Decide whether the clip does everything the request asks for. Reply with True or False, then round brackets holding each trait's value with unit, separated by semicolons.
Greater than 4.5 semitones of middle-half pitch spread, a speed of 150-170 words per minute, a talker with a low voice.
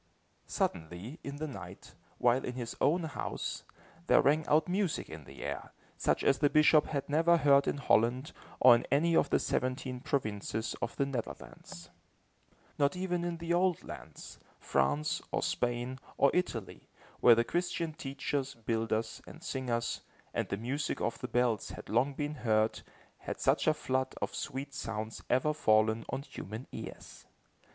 True (4.9 semitones; 160 wpm; 130 Hz)